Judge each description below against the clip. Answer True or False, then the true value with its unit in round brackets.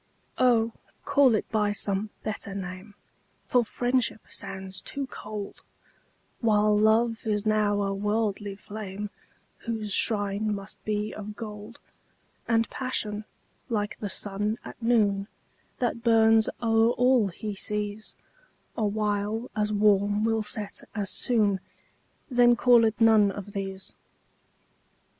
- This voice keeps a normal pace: False (120 wpm)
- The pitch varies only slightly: True (1.7 semitones)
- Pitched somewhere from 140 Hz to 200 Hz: False (210 Hz)